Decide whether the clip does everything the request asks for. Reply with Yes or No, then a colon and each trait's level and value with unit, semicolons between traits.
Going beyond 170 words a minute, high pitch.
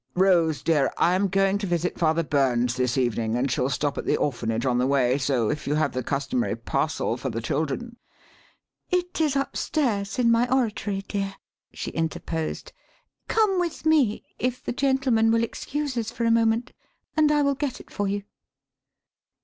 Yes: average, 180 wpm; high, 195 Hz